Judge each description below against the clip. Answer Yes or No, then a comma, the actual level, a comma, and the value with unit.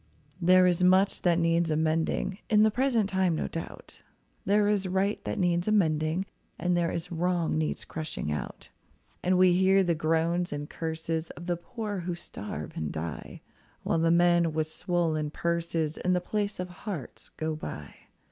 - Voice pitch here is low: No, medium, 175 Hz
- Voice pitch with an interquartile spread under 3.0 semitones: Yes, narrow, 2.5 semitones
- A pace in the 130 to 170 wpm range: Yes, average, 165 wpm